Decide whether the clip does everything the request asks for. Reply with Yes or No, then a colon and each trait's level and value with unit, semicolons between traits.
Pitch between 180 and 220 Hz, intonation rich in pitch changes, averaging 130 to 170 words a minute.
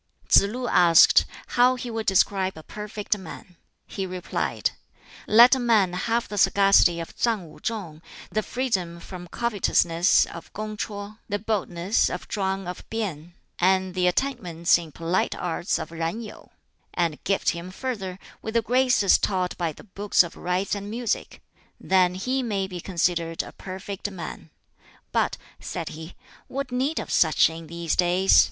No: high, 190 Hz; average, 3.8 semitones; average, 160 wpm